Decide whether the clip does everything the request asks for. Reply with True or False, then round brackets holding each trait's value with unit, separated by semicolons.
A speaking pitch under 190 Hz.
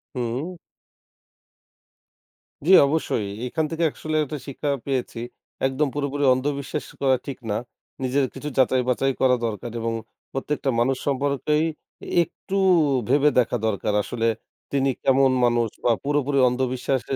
True (135 Hz)